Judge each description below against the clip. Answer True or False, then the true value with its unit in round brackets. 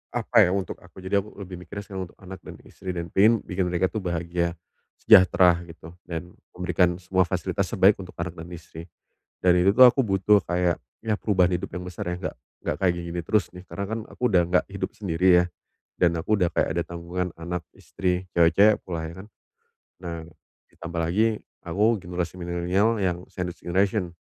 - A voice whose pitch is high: False (90 Hz)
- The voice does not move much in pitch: True (2.0 semitones)